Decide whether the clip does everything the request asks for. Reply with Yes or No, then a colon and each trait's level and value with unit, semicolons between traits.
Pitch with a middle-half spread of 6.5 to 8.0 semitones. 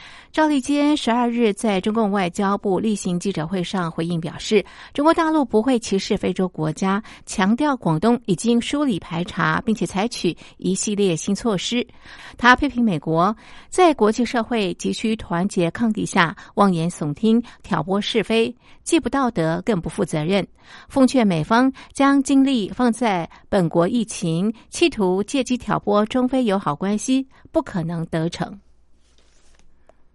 No: wide, 5.4 semitones